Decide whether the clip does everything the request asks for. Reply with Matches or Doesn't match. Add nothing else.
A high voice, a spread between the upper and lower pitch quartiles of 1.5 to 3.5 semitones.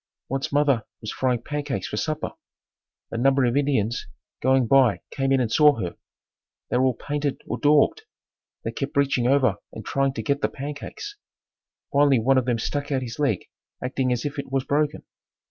Doesn't match